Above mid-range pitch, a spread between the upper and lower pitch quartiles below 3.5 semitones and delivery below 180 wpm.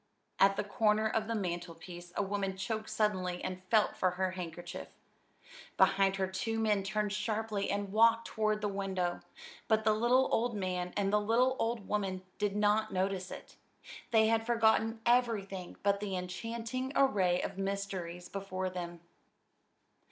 Yes: high, 200 Hz; average, 2.9 semitones; average, 155 wpm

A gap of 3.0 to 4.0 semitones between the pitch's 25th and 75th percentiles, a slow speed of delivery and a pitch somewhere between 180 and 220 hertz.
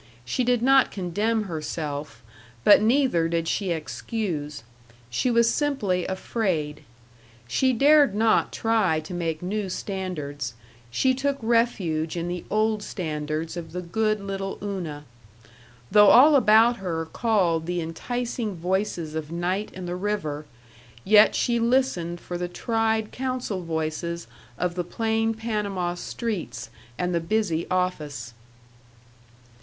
No: average, 5.2 semitones; slow, 130 wpm; medium, 185 Hz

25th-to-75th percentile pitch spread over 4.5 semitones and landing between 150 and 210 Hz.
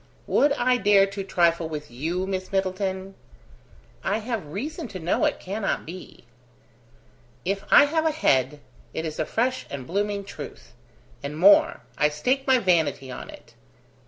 Yes: wide, 5.5 semitones; high, 190 Hz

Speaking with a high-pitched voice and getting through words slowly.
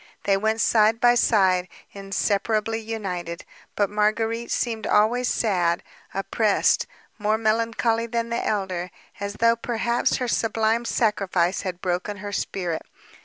Yes: high, 215 Hz; slow, 125 wpm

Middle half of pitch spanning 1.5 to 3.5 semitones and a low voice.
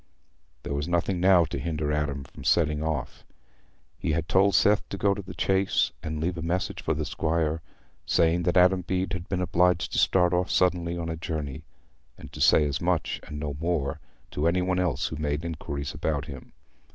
Yes: average, 3.2 semitones; very low, 85 Hz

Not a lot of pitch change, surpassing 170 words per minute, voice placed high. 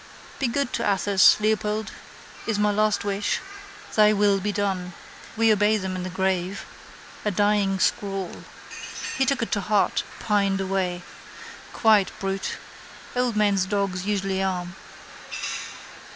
No: narrow, 1.7 semitones; slow, 135 wpm; high, 200 Hz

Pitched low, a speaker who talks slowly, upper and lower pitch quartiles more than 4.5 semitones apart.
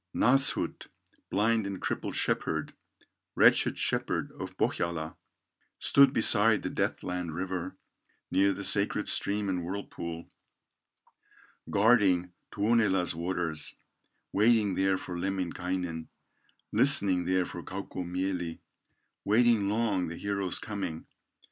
No: very low, 95 Hz; slow, 105 wpm; narrow, 2.6 semitones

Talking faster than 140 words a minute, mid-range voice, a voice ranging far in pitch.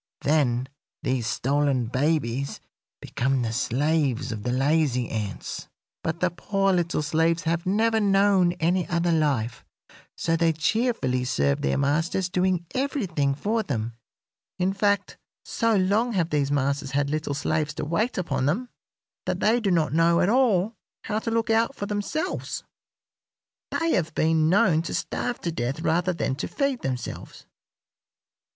Yes: average, 150 wpm; medium, 165 Hz; wide, 6.0 semitones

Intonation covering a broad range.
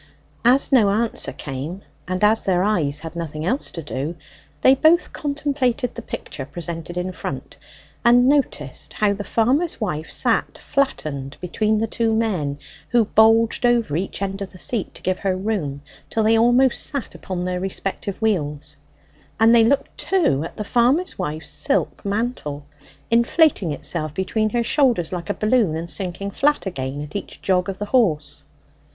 Yes: wide, 6.1 semitones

